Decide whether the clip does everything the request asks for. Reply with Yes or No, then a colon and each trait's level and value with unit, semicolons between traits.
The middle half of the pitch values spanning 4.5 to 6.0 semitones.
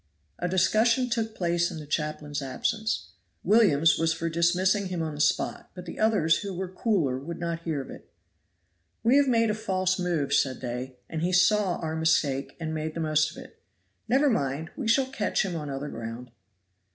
Yes: average, 5.3 semitones